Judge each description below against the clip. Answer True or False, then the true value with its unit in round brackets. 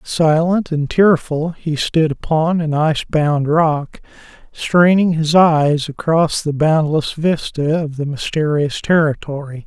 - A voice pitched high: False (155 Hz)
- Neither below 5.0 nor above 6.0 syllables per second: False (3.8 syllables/s)